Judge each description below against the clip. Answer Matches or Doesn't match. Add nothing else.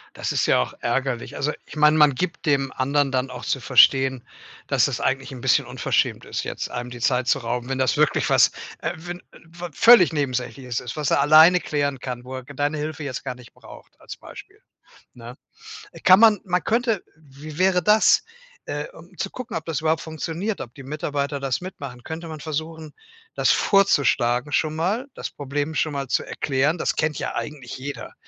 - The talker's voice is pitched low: Doesn't match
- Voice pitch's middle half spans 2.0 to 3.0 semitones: Doesn't match